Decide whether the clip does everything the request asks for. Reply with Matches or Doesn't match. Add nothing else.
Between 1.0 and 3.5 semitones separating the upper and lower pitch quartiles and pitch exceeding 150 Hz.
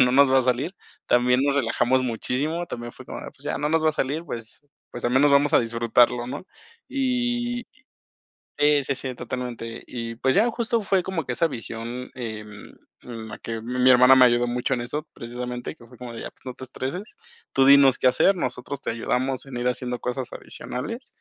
Doesn't match